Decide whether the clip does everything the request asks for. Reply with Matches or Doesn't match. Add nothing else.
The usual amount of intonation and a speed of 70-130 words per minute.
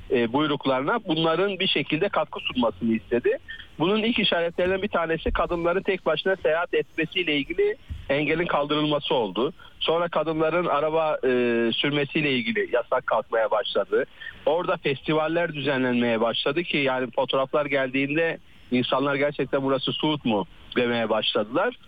Matches